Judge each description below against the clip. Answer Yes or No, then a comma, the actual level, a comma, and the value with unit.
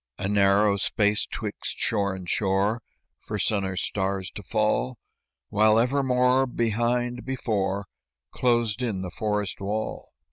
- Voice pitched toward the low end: Yes, low, 105 Hz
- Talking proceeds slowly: Yes, slow, 130 wpm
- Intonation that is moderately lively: Yes, average, 3.2 semitones